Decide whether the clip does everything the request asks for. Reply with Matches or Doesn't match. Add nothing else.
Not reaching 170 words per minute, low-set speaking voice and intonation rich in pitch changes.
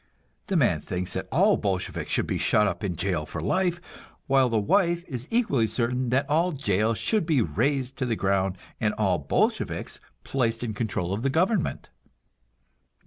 Doesn't match